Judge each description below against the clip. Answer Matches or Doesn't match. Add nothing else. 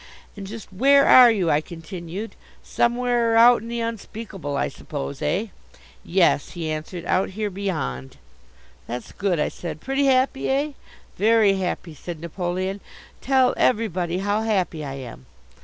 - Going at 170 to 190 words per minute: Doesn't match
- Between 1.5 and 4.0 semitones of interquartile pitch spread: Doesn't match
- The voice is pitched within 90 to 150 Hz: Doesn't match